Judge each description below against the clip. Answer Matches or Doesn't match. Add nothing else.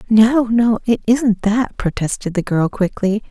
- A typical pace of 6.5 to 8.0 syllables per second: Doesn't match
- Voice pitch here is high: Matches